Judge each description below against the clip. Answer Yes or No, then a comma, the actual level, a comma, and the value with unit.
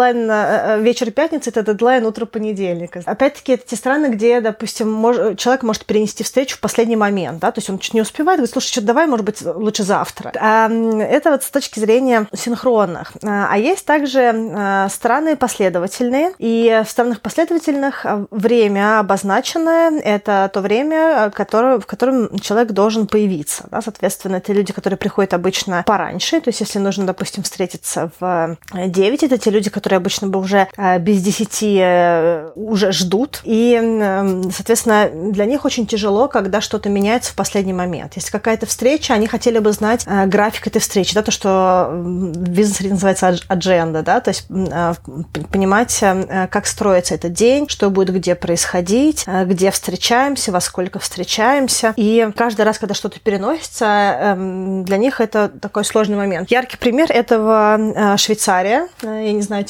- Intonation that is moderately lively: Yes, average, 3.4 semitones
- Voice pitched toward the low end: No, high, 215 Hz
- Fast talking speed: Yes, fast, 165 wpm